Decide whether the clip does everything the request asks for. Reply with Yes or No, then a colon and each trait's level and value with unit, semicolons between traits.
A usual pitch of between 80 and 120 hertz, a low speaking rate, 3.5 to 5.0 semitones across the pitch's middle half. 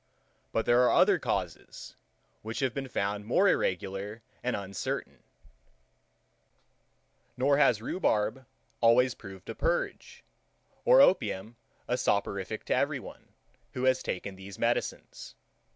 Yes: low, 115 Hz; slow, 120 wpm; average, 4.6 semitones